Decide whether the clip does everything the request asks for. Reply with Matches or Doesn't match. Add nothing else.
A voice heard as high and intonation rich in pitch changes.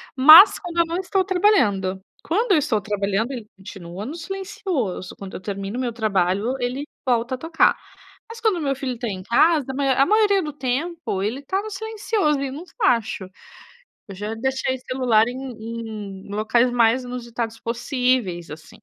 Matches